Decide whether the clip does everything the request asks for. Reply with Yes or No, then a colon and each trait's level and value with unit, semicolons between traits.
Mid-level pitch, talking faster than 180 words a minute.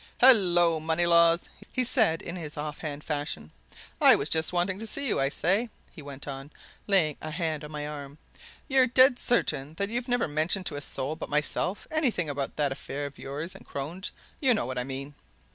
Yes: medium, 160 Hz; average, 200 wpm